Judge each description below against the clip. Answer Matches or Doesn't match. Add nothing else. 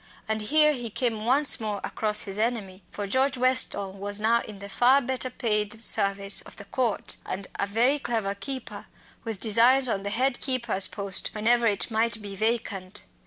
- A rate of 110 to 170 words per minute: Doesn't match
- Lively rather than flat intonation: Doesn't match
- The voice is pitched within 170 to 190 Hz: Doesn't match